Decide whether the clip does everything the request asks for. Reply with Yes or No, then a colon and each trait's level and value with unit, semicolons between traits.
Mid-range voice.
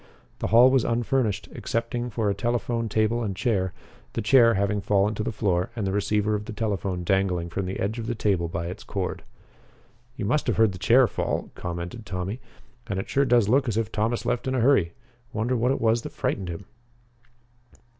No: low, 110 Hz